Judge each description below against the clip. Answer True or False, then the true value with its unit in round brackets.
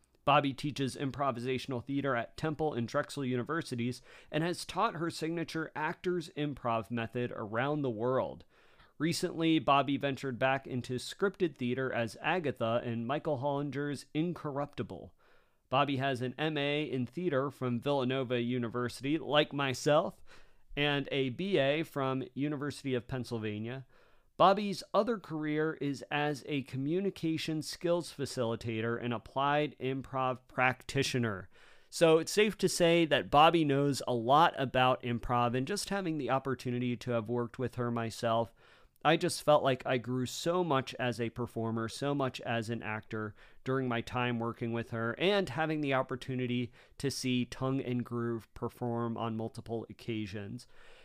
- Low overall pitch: True (130 Hz)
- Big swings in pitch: False (3.6 semitones)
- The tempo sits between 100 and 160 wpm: True (145 wpm)